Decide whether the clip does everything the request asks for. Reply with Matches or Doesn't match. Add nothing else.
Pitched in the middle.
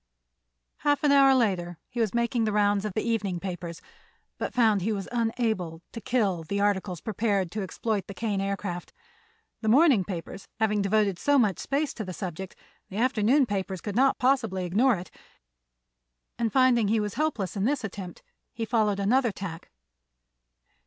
Doesn't match